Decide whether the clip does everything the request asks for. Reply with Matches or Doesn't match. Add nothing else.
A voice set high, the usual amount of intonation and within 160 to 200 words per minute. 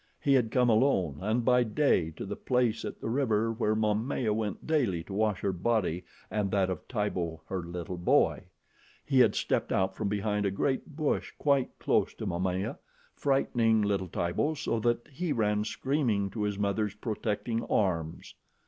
Doesn't match